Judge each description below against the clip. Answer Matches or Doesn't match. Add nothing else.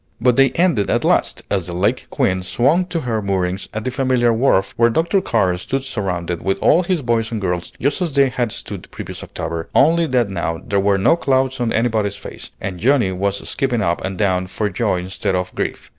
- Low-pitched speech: Matches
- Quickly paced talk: Matches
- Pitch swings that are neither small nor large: Doesn't match